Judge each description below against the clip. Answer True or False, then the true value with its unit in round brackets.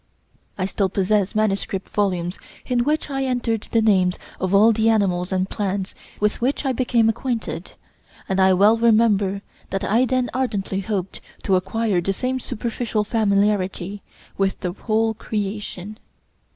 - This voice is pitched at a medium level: False (210 Hz)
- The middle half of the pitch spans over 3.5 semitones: False (2.9 semitones)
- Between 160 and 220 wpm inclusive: False (150 wpm)